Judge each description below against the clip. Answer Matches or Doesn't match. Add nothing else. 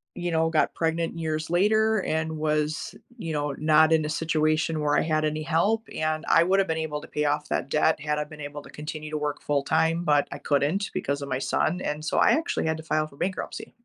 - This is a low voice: Doesn't match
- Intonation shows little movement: Matches